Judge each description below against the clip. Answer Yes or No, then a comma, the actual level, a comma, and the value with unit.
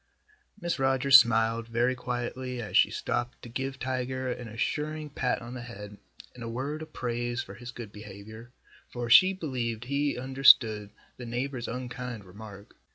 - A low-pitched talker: Yes, low, 120 Hz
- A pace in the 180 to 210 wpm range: No, average, 160 wpm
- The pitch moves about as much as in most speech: No, narrow, 2.3 semitones